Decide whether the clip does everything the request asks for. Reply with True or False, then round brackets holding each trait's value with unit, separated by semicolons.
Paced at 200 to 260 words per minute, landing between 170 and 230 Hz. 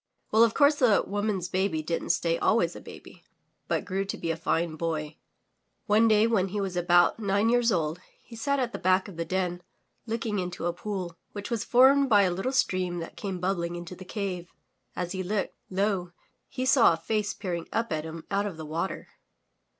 True (205 wpm; 190 Hz)